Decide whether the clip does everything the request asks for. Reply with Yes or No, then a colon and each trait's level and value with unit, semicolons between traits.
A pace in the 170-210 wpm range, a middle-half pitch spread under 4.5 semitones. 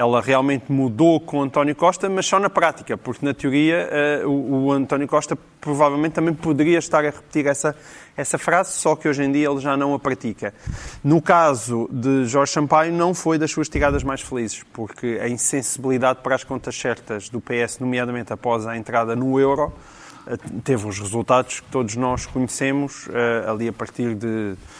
Yes: average, 180 wpm; average, 4.0 semitones